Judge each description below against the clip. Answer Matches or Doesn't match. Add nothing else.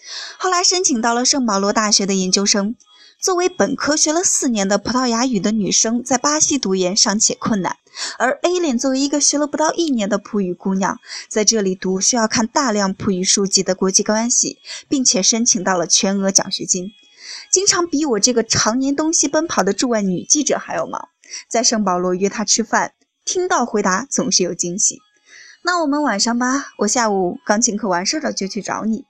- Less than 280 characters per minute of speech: Doesn't match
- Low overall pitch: Doesn't match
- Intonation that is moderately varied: Doesn't match